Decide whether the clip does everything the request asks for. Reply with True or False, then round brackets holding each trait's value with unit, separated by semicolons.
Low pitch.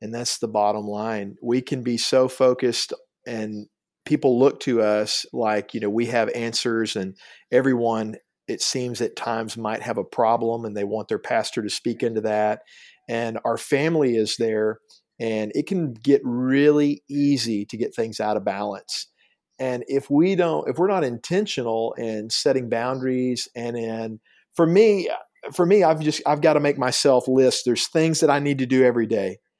True (120 Hz)